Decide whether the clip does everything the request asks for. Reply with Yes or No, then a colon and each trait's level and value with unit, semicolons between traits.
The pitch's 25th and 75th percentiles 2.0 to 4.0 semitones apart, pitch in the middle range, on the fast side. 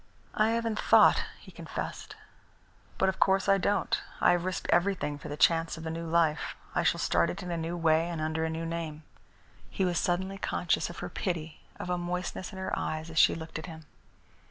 Yes: narrow, 2.5 semitones; medium, 170 Hz; fast, 215 wpm